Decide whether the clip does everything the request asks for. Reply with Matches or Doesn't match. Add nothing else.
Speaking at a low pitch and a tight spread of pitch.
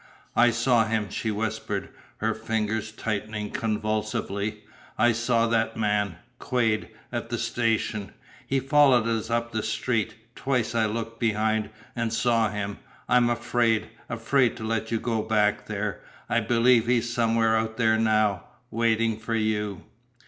Matches